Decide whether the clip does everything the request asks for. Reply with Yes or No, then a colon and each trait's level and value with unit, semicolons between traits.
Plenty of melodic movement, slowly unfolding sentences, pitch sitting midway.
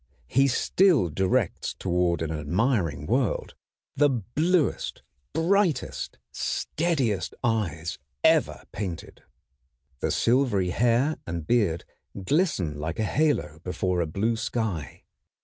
No: wide, 8.0 semitones; slow, 105 wpm; low, 105 Hz